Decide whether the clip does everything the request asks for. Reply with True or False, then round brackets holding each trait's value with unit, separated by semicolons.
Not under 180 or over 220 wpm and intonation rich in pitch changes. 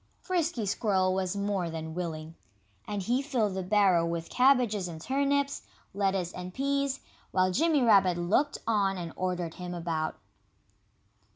False (145 wpm; 5.9 semitones)